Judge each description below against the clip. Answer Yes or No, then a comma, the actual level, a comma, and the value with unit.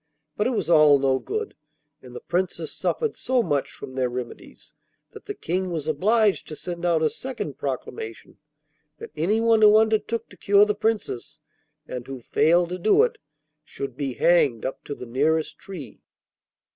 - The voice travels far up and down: Yes, wide, 7.5 semitones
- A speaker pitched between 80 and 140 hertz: No, medium, 170 Hz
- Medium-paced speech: Yes, average, 170 wpm